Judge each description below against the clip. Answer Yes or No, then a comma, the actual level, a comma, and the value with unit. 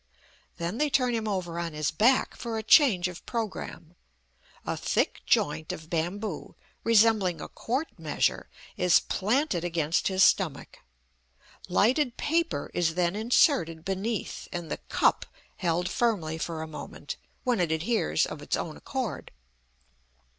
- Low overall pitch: No, high, 190 Hz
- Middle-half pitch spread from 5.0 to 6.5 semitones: Yes, wide, 5.5 semitones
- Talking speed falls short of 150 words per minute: Yes, average, 140 wpm